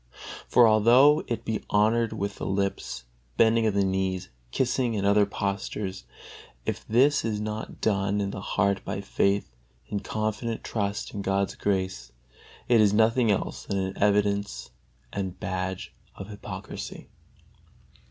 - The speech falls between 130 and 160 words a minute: Yes, average, 140 wpm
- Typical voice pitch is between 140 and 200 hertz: No, low, 100 Hz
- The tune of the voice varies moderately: No, narrow, 2.2 semitones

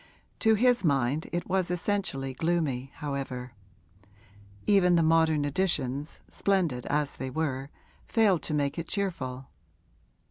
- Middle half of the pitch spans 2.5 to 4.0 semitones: No, average, 5.0 semitones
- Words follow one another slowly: Yes, slow, 120 wpm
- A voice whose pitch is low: No, medium, 155 Hz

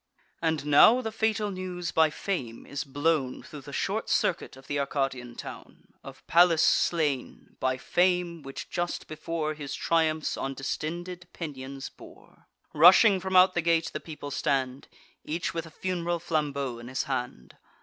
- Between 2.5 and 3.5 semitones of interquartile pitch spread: No, average, 4.2 semitones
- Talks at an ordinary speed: Yes, average, 155 wpm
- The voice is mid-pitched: Yes, medium, 155 Hz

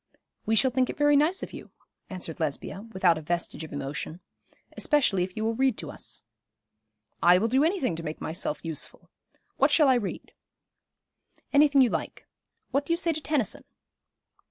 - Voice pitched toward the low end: No, high, 225 Hz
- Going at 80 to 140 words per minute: No, average, 180 wpm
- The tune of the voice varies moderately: No, wide, 8.8 semitones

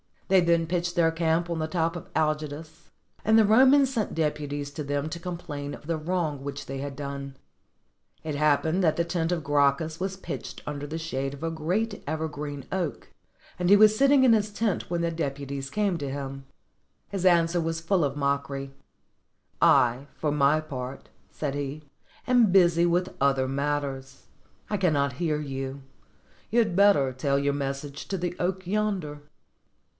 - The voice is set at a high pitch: No, medium, 155 Hz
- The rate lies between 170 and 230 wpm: Yes, average, 180 wpm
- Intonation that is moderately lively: Yes, average, 4.0 semitones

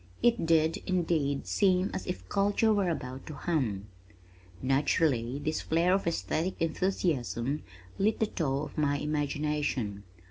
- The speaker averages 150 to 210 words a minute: No, slow, 135 wpm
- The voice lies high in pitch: No, medium, 155 Hz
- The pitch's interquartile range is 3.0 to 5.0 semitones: Yes, average, 4.7 semitones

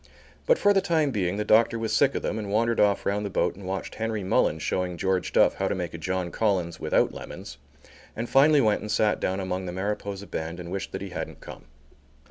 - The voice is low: Yes, low, 100 Hz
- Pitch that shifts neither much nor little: Yes, average, 3.3 semitones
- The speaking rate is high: Yes, fast, 235 wpm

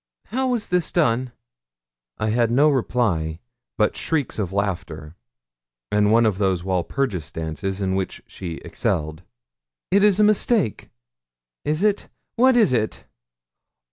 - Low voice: Yes, low, 110 Hz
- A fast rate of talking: No, slow, 135 wpm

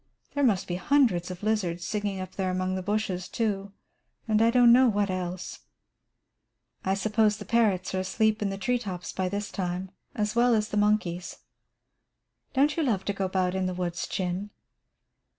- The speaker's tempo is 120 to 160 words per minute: No, average, 185 wpm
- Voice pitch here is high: Yes, high, 200 Hz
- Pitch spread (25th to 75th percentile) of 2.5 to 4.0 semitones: Yes, average, 2.9 semitones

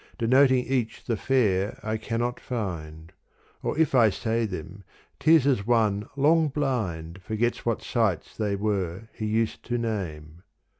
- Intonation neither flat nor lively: Yes, average, 4.0 semitones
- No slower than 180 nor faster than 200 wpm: No, average, 150 wpm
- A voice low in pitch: Yes, low, 110 Hz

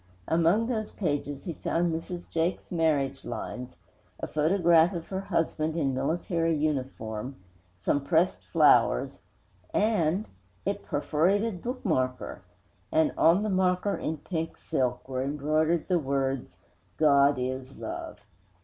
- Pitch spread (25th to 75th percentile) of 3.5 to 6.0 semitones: Yes, average, 4.4 semitones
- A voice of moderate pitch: Yes, medium, 160 Hz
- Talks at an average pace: No, slow, 120 wpm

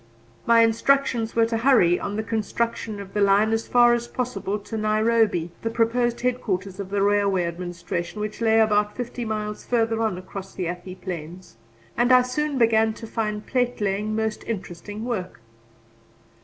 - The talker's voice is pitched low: No, high, 215 Hz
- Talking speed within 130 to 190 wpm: Yes, average, 165 wpm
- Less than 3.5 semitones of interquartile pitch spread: Yes, average, 2.9 semitones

